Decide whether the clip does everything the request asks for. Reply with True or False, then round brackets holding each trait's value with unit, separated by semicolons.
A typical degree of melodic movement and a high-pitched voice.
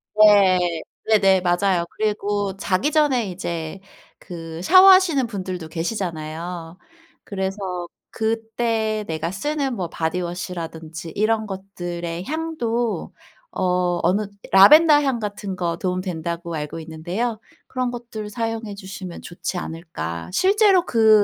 True (4.6 semitones; 195 Hz)